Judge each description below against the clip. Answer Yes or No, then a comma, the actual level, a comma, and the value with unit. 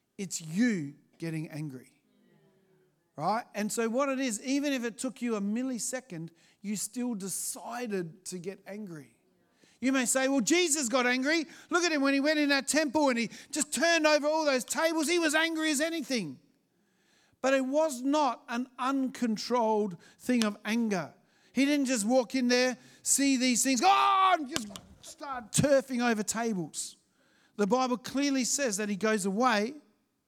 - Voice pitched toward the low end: No, very high, 250 Hz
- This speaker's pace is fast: No, average, 170 wpm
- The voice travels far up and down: No, average, 4.9 semitones